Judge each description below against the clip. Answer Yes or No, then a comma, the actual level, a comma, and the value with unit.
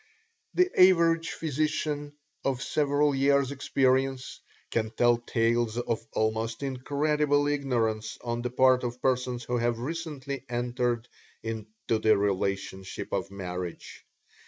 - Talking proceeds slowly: Yes, slow, 115 wpm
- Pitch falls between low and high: No, low, 125 Hz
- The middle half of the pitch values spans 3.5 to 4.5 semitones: Yes, average, 3.8 semitones